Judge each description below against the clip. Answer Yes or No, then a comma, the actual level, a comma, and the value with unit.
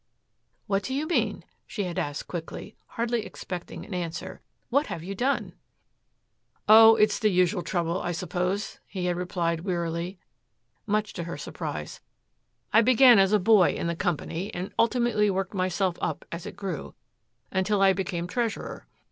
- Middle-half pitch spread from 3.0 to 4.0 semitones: Yes, average, 3.5 semitones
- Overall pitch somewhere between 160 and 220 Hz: Yes, high, 190 Hz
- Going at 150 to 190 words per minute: Yes, average, 165 wpm